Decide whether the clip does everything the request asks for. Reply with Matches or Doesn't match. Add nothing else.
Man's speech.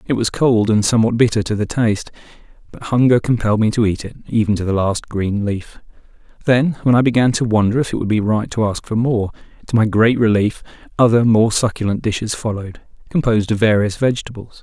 Matches